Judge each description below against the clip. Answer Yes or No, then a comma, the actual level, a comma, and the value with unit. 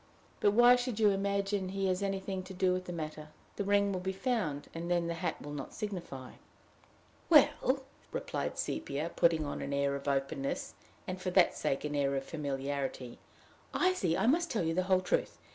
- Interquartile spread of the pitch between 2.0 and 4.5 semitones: No, wide, 5.5 semitones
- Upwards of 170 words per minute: Yes, average, 200 wpm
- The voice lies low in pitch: No, medium, 185 Hz